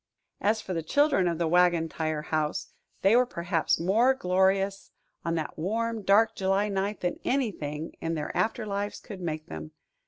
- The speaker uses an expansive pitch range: No, average, 4.4 semitones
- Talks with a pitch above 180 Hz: Yes, high, 190 Hz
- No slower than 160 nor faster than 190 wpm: Yes, average, 175 wpm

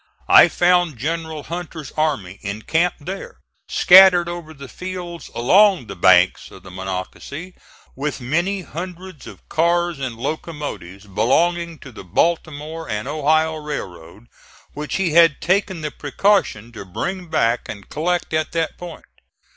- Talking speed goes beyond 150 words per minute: No, average, 140 wpm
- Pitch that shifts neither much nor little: No, wide, 6.6 semitones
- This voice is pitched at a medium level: Yes, medium, 155 Hz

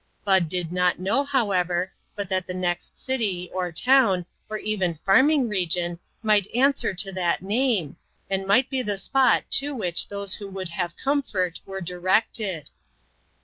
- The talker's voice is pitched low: No, high, 195 Hz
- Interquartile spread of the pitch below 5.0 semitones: Yes, average, 4.0 semitones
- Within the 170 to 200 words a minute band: No, average, 155 wpm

